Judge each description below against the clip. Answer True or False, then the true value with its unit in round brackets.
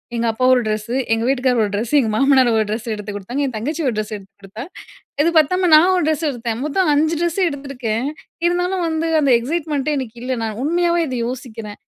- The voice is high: True (260 Hz)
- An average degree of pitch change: False (5.8 semitones)